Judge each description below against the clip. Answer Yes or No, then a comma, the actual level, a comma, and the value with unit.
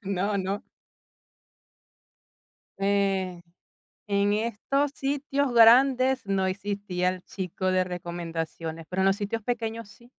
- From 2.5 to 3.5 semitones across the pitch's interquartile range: No, average, 3.9 semitones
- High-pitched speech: Yes, high, 200 Hz